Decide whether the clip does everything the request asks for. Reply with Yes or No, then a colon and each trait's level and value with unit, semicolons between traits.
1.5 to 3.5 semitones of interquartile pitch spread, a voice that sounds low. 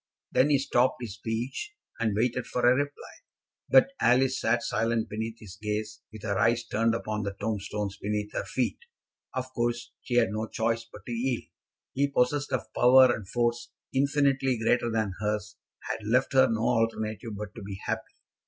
Yes: average, 2.8 semitones; low, 115 Hz